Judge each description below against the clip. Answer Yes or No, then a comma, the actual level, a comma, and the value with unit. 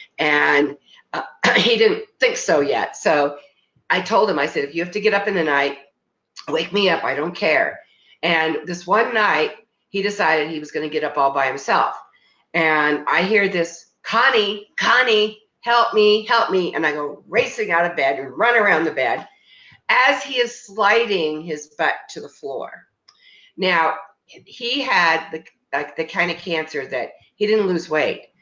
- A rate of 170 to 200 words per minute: Yes, average, 185 wpm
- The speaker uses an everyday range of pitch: No, wide, 6.0 semitones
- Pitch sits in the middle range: Yes, medium, 180 Hz